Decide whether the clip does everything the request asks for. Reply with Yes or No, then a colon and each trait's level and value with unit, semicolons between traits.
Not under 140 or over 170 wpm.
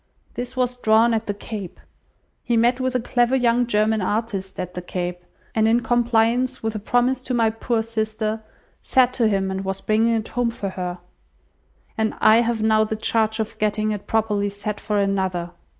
No: average, 190 wpm